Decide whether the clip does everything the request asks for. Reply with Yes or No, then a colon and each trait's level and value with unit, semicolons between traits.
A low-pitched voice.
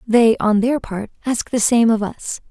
No: high, 225 Hz